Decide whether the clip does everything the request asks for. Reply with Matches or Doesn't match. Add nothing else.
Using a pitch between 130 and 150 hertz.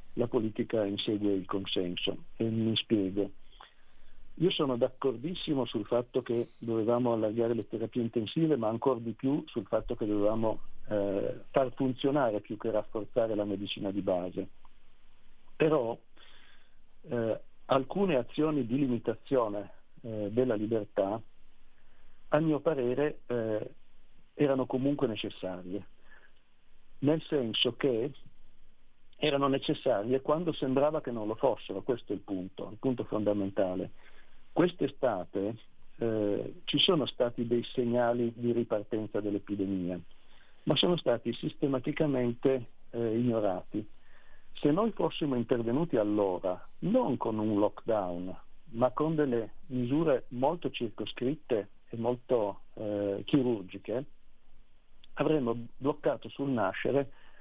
Doesn't match